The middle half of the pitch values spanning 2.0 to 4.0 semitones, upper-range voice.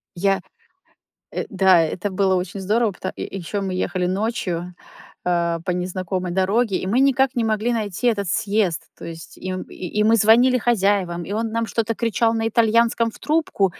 Yes: average, 3.7 semitones; high, 200 Hz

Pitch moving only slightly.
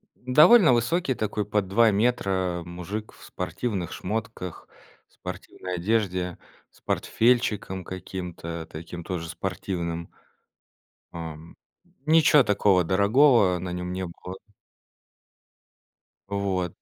No: average, 4.0 semitones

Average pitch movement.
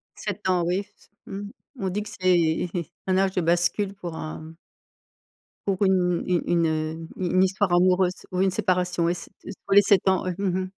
No: narrow, 1.7 semitones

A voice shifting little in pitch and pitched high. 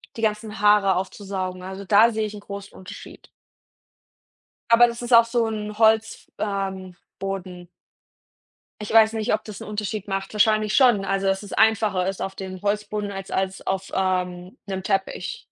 Yes: narrow, 2.1 semitones; high, 200 Hz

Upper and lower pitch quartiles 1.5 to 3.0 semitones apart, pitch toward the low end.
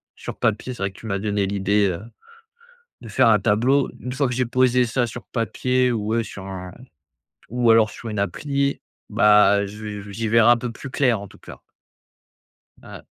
No: average, 3.4 semitones; low, 115 Hz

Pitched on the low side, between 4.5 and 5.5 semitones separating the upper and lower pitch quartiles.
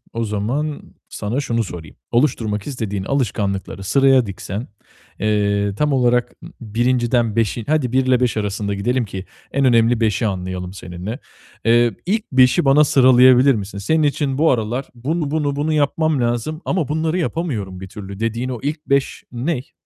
Yes: low, 120 Hz; average, 5.0 semitones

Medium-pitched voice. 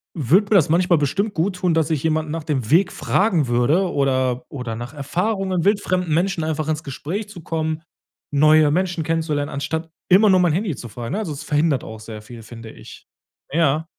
Yes: medium, 160 Hz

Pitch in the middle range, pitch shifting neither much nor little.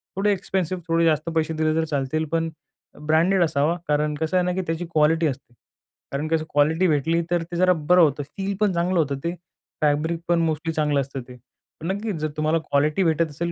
No: medium, 160 Hz; narrow, 2.3 semitones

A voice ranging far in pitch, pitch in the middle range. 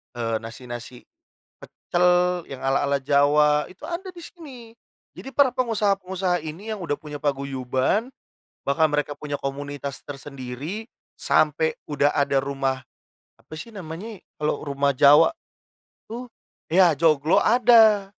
Yes: wide, 6.1 semitones; medium, 150 Hz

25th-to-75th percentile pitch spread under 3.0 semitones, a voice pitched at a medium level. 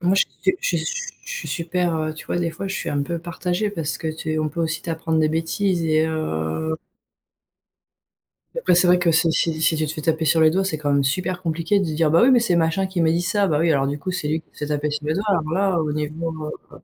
Yes: narrow, 2.5 semitones; medium, 165 Hz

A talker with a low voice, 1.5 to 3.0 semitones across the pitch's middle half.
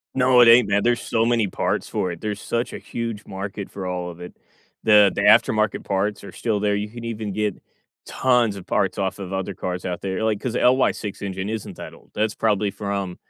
Yes: low, 105 Hz; narrow, 2.6 semitones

